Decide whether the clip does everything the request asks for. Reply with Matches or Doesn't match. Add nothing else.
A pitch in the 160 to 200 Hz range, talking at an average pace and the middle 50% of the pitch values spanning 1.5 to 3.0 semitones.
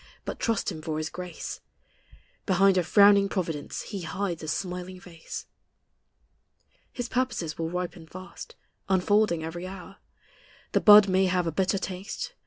Matches